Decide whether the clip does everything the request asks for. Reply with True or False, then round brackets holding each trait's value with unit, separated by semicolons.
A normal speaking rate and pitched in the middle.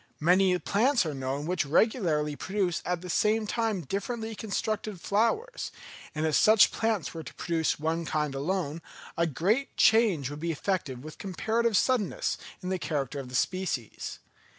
True (160 wpm; 180 Hz)